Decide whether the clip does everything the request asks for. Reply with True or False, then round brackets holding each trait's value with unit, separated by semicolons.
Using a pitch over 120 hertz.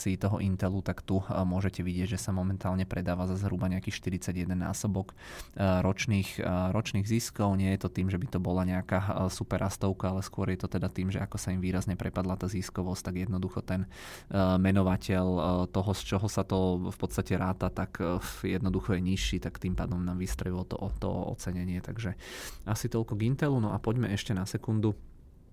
False (95 Hz)